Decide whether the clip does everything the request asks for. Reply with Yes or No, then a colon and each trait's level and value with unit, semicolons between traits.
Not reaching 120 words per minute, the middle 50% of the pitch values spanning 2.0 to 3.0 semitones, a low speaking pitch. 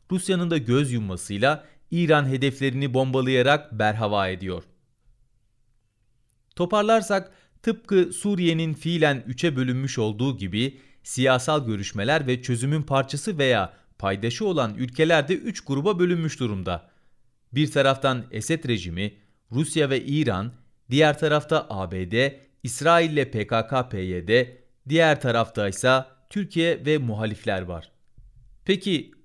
No: average, 105 wpm; wide, 5.5 semitones; low, 130 Hz